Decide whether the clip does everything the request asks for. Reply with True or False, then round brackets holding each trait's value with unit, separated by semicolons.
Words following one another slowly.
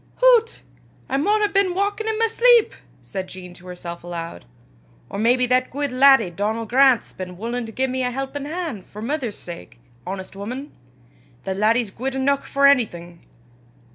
False (175 wpm)